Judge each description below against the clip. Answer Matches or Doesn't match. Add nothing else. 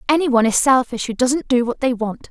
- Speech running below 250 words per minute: Doesn't match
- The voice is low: Doesn't match